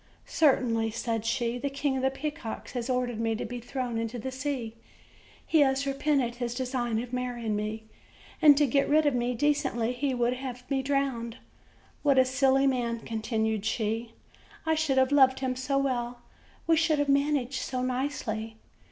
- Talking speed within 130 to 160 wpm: No, average, 180 wpm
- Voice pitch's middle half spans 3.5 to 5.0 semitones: No, average, 2.8 semitones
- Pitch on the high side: Yes, very high, 255 Hz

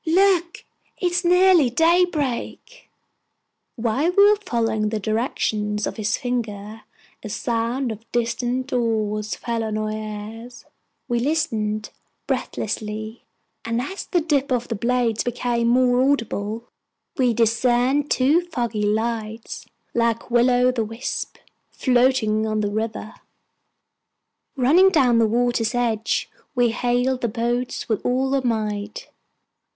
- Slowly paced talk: Yes, slow, 125 wpm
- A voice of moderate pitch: No, high, 240 Hz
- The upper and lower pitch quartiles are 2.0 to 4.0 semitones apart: Yes, average, 3.0 semitones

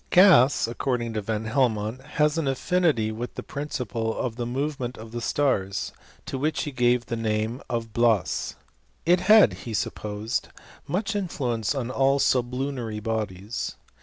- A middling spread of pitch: Yes, average, 4.0 semitones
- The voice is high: No, low, 120 Hz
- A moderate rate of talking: Yes, average, 155 wpm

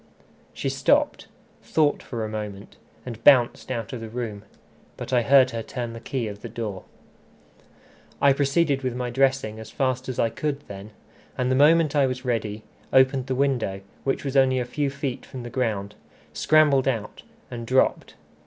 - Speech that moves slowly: No, average, 180 wpm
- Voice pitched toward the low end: Yes, low, 125 Hz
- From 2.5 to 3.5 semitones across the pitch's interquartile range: Yes, average, 3.2 semitones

